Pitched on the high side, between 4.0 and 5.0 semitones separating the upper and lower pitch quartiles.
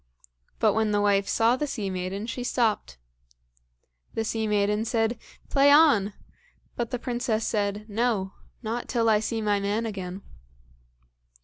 No: high, 220 Hz; narrow, 2.6 semitones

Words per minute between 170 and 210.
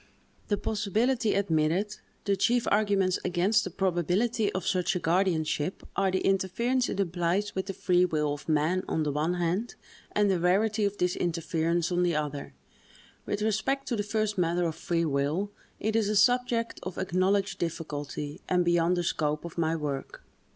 Yes: average, 175 wpm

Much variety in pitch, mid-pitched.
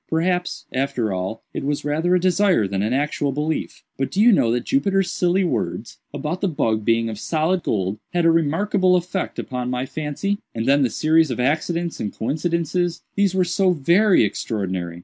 Yes: wide, 6.9 semitones; medium, 155 Hz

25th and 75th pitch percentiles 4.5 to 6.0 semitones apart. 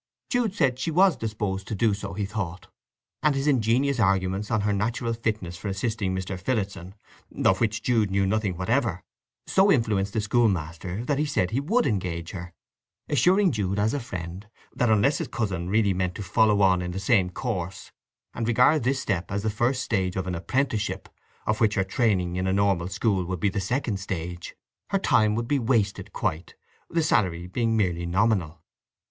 No: average, 4.1 semitones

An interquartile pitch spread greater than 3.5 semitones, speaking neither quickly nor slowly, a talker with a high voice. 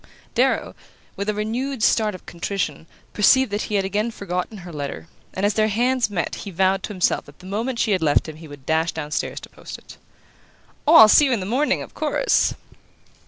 No: average, 4.3 semitones; fast, 215 wpm; high, 200 Hz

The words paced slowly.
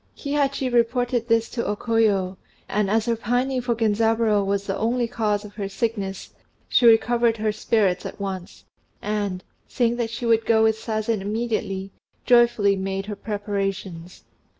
No: average, 155 wpm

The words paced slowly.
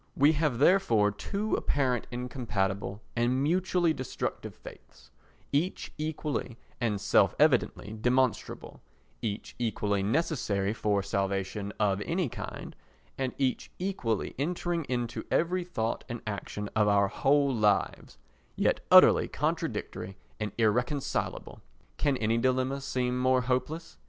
Yes: slow, 120 wpm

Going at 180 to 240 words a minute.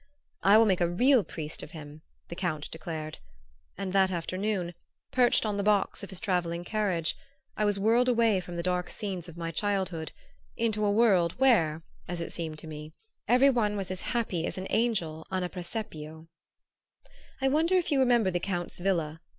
Yes: average, 190 wpm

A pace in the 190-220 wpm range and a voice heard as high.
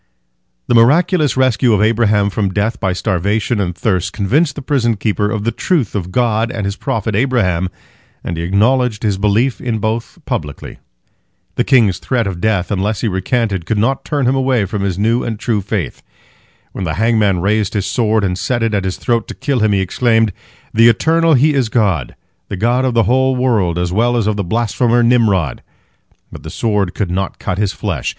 No: average, 200 wpm; low, 110 Hz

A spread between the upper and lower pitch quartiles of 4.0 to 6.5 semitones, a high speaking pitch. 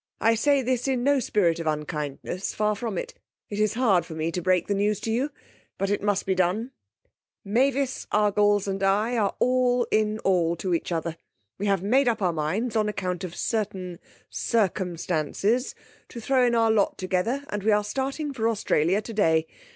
Yes: average, 4.3 semitones; high, 205 Hz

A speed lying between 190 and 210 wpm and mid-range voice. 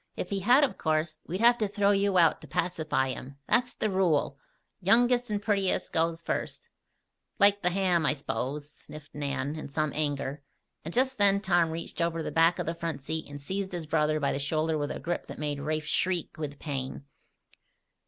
Yes: fast, 205 wpm; medium, 165 Hz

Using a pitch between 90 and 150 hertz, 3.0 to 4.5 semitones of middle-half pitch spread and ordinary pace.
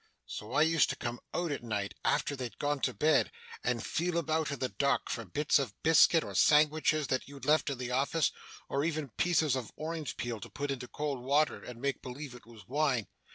No: medium, 140 Hz; average, 3.8 semitones; fast, 215 wpm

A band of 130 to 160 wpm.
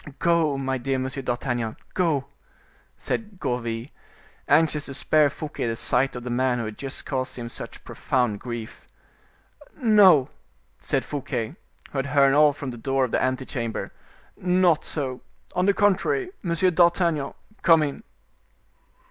Yes: average, 150 wpm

